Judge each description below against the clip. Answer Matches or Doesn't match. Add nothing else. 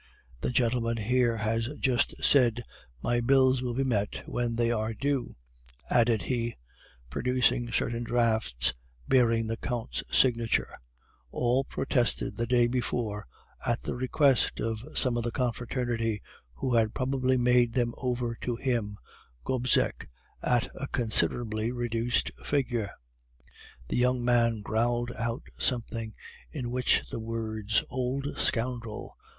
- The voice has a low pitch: Matches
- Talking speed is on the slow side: Matches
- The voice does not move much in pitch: Matches